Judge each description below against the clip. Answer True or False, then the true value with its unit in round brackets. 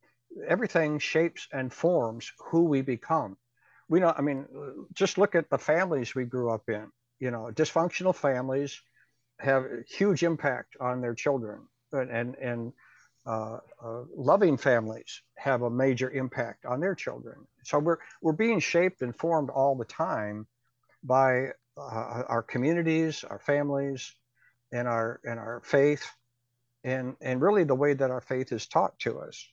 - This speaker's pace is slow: False (155 wpm)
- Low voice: True (130 Hz)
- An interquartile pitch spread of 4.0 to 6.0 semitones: True (4.4 semitones)